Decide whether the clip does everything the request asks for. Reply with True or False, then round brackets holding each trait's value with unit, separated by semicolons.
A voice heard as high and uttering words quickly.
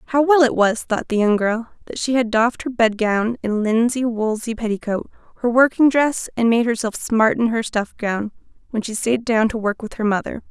True (230 Hz; 225 wpm)